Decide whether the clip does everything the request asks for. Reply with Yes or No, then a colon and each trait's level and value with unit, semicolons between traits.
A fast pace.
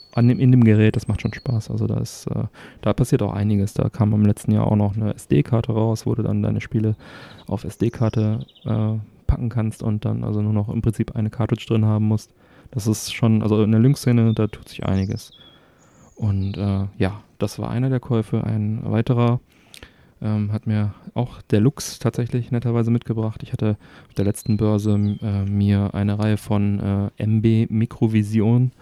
Yes: fast, 195 wpm